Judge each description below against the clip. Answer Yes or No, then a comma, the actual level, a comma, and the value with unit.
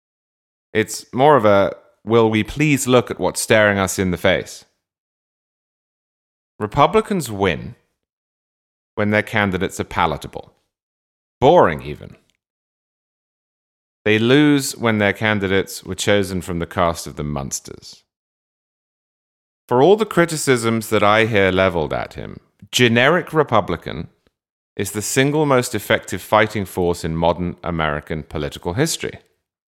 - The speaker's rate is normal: No, slow, 125 wpm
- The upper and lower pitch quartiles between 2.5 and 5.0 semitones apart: No, wide, 5.4 semitones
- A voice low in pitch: Yes, low, 105 Hz